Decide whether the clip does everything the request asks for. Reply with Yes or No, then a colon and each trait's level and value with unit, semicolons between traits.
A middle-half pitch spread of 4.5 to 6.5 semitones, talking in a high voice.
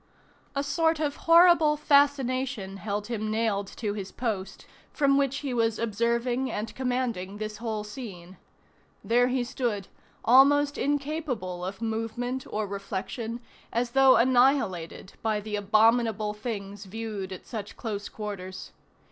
No: average, 4.1 semitones; high, 230 Hz